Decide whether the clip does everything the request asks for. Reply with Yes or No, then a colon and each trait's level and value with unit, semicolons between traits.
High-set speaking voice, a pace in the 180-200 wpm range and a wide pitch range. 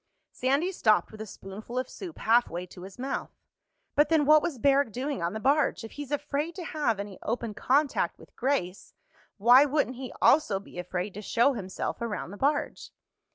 Yes: very high, 250 Hz; average, 190 wpm; wide, 5.7 semitones